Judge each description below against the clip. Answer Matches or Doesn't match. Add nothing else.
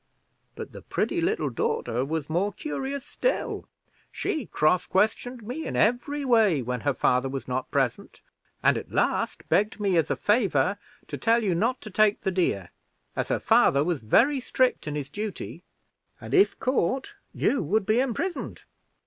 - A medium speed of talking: Matches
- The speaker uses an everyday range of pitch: Doesn't match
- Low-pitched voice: Doesn't match